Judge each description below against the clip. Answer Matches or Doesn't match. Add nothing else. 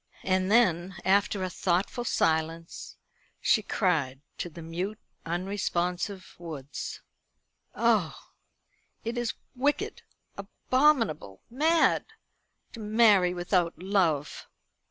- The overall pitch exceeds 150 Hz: Matches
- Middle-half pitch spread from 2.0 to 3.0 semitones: Doesn't match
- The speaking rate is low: Matches